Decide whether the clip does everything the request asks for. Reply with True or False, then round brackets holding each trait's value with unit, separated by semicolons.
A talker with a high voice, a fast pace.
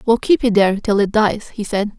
True (215 Hz; 275 wpm)